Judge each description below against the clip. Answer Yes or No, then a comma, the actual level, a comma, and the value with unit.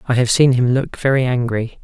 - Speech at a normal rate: No, fast, 230 wpm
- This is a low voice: Yes, low, 125 Hz